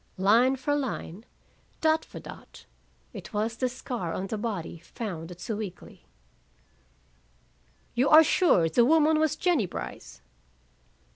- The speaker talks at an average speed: No, slow, 130 wpm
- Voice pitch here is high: Yes, high, 230 Hz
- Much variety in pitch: Yes, wide, 7.5 semitones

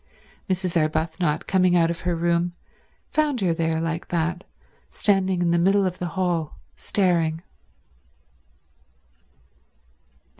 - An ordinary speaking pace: No, slow, 115 wpm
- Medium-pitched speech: Yes, medium, 175 Hz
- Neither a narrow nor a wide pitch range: No, narrow, 2.0 semitones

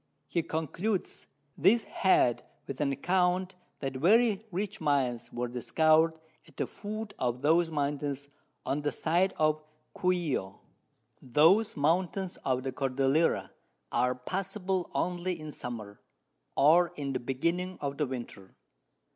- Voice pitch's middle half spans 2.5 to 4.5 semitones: No, wide, 5.4 semitones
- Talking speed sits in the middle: No, slow, 130 wpm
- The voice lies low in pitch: No, medium, 155 Hz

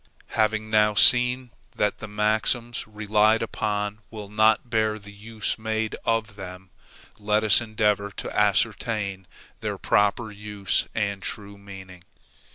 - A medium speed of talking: No, slow, 130 wpm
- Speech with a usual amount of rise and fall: No, narrow, 1.4 semitones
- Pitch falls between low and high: No, low, 105 Hz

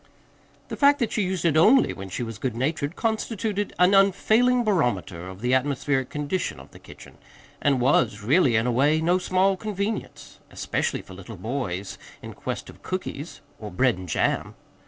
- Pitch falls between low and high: Yes, medium, 145 Hz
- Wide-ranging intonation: Yes, wide, 8.8 semitones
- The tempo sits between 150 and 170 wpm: No, average, 180 wpm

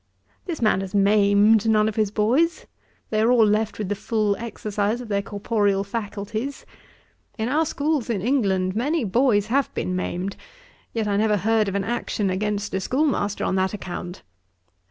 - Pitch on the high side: Yes, high, 210 Hz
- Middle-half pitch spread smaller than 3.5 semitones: Yes, narrow, 2.5 semitones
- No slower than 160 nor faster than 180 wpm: Yes, average, 175 wpm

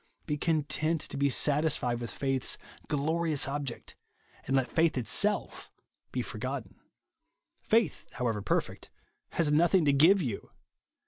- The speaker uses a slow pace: Yes, slow, 130 wpm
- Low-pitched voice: No, medium, 145 Hz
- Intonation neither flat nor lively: Yes, average, 3.5 semitones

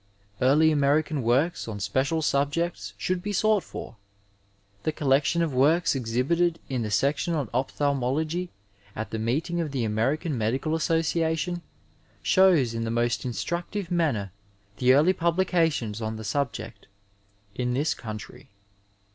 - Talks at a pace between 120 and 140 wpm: Yes, slow, 135 wpm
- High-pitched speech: No, medium, 140 Hz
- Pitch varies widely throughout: Yes, wide, 5.9 semitones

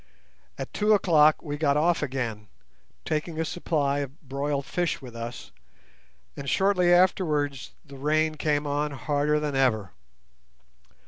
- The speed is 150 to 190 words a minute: No, slow, 135 wpm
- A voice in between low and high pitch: Yes, medium, 150 Hz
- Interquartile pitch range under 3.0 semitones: Yes, narrow, 2.4 semitones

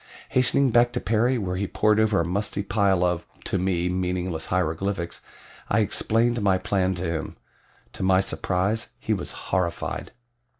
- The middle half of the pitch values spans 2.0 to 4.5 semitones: Yes, average, 3.1 semitones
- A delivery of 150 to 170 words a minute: Yes, average, 160 wpm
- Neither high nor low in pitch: No, very low, 95 Hz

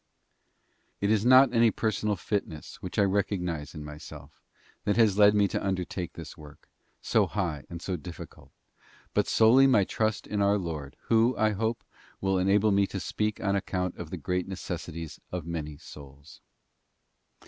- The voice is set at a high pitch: No, very low, 95 Hz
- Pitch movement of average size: Yes, average, 4.3 semitones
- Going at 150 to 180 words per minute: Yes, average, 165 wpm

